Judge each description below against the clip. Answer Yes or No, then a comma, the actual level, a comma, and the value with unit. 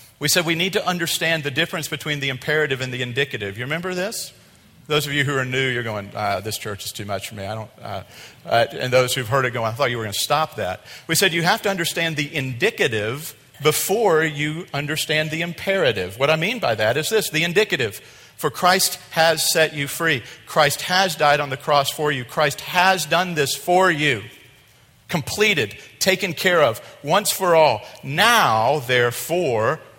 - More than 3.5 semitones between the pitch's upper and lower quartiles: Yes, average, 4.8 semitones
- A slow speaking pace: No, fast, 205 wpm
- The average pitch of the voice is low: No, medium, 150 Hz